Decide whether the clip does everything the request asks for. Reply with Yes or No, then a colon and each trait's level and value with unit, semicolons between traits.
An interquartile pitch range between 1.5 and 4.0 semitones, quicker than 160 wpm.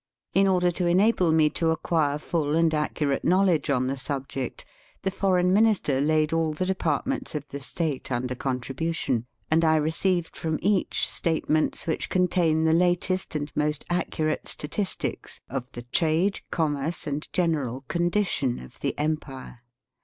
No: average, 3.7 semitones; average, 155 wpm